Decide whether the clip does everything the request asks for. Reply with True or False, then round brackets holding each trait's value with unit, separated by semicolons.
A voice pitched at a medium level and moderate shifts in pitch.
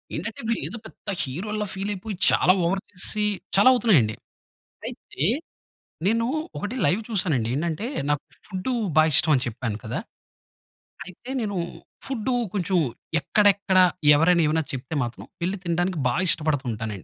False (180 Hz; 5.9 semitones)